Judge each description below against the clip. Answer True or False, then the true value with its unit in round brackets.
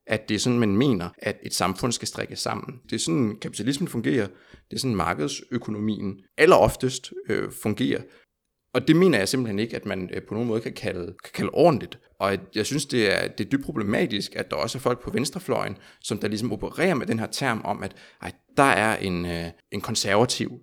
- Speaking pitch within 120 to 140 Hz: False (110 Hz)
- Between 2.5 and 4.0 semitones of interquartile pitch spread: False (4.5 semitones)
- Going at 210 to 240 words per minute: True (220 wpm)